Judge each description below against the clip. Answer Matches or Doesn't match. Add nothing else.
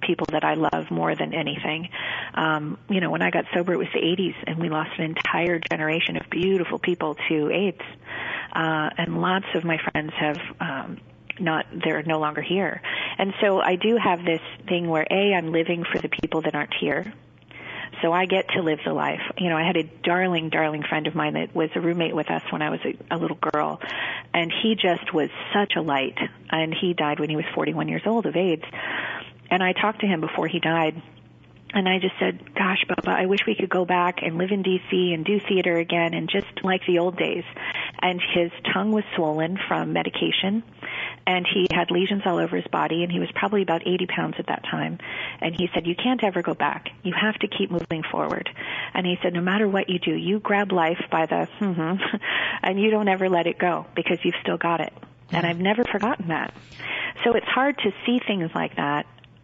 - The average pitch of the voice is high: Doesn't match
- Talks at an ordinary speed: Doesn't match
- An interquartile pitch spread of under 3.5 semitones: Matches